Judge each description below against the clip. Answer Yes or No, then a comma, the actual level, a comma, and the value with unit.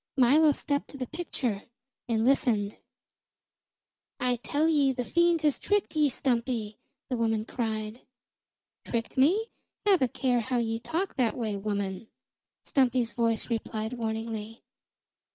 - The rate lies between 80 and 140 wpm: Yes, slow, 135 wpm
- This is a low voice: No, high, 245 Hz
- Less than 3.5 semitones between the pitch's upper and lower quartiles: No, average, 4.0 semitones